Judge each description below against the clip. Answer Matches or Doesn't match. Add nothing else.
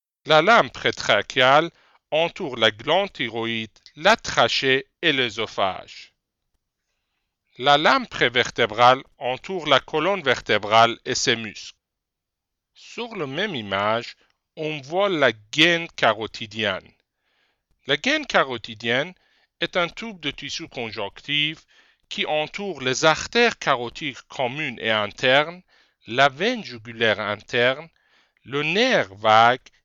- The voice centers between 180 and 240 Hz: Doesn't match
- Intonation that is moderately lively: Doesn't match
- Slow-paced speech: Matches